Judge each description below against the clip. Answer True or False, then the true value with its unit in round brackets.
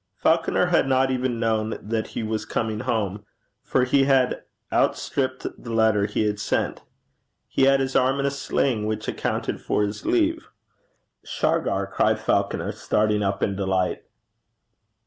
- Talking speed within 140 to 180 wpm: True (150 wpm)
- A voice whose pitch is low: True (115 Hz)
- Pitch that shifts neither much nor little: True (3.9 semitones)